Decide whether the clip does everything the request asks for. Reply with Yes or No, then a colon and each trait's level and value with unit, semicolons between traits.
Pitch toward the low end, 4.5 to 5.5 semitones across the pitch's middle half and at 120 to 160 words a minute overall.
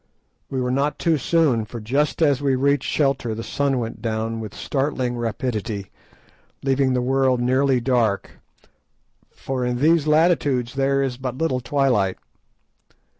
No: low, 130 Hz; average, 2.7 semitones; average, 145 wpm